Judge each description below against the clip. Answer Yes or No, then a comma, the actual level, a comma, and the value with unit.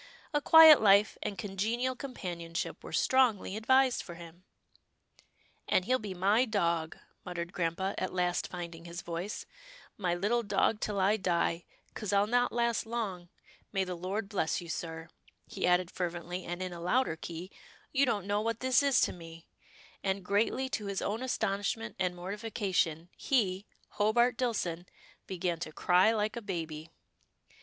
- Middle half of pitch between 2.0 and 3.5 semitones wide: No, average, 4.3 semitones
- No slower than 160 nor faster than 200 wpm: Yes, average, 165 wpm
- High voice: Yes, high, 195 Hz